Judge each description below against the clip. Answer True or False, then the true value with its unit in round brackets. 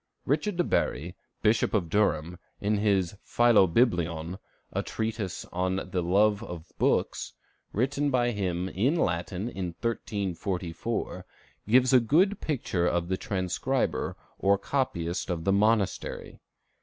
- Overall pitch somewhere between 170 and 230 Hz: False (100 Hz)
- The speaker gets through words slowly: True (125 wpm)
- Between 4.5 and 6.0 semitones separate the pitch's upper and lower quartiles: True (5.0 semitones)